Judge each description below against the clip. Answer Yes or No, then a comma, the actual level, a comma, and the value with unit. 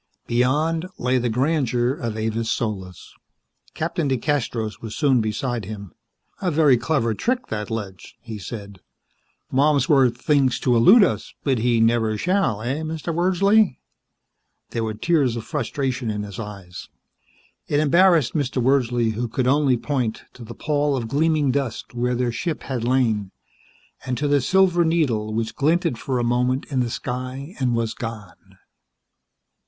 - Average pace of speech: Yes, average, 155 wpm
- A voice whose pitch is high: No, low, 125 Hz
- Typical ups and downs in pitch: Yes, average, 4.6 semitones